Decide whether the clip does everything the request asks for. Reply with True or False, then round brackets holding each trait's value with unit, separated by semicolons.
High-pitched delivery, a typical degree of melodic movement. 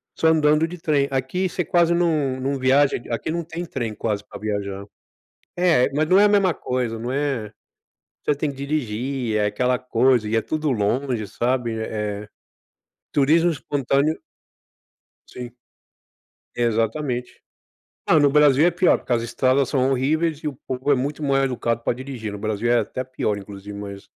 False (130 Hz; 4.7 semitones)